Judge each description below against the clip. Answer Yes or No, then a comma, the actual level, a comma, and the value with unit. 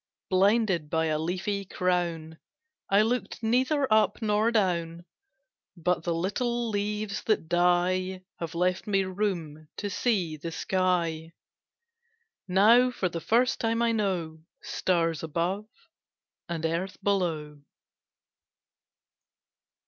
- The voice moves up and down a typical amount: Yes, average, 4.0 semitones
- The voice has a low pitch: No, medium, 185 Hz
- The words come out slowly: Yes, slow, 110 wpm